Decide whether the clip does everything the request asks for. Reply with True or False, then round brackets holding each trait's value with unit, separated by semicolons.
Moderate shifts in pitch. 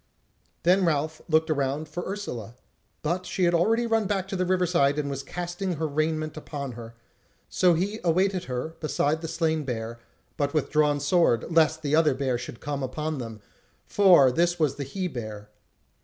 True (4.2 semitones)